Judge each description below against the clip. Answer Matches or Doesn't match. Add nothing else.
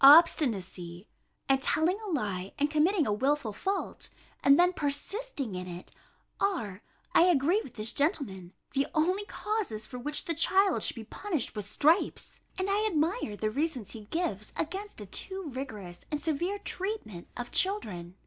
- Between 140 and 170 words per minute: Matches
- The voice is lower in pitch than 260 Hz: Doesn't match